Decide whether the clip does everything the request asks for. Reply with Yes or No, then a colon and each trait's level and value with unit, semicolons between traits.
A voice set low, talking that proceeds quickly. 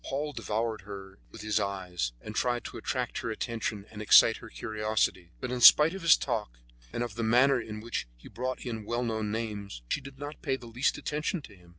Yes: low, 115 Hz; fast, 220 wpm